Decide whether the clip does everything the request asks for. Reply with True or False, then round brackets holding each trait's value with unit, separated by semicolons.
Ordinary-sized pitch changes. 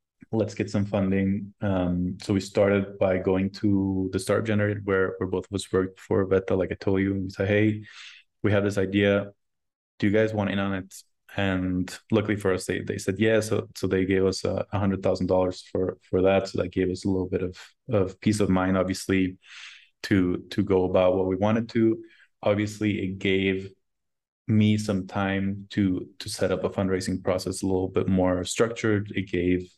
False (1.7 semitones)